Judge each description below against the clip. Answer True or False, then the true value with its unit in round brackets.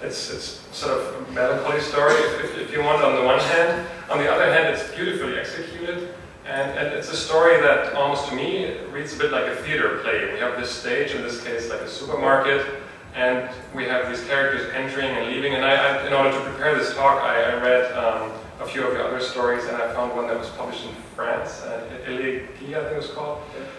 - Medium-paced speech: False (225 wpm)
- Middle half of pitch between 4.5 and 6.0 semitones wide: True (5.0 semitones)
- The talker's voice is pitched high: False (140 Hz)